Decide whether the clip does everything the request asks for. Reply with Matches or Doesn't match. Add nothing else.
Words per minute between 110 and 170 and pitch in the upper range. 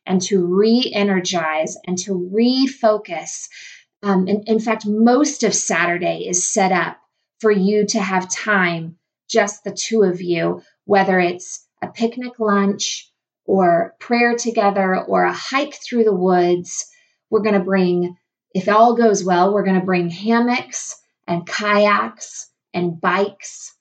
Matches